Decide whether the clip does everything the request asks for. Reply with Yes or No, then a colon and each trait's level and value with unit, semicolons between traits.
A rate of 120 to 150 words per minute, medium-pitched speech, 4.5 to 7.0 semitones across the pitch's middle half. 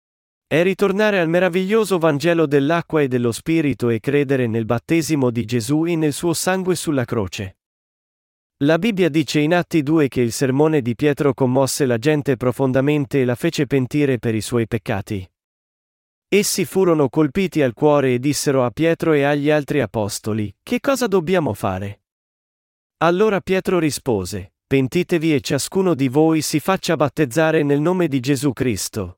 No: average, 160 wpm; medium, 145 Hz; average, 5.0 semitones